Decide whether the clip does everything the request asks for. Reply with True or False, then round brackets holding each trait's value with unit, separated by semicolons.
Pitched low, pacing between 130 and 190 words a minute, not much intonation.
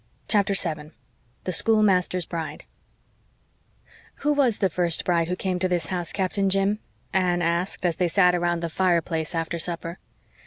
False (180 Hz; 155 wpm; 2.2 semitones)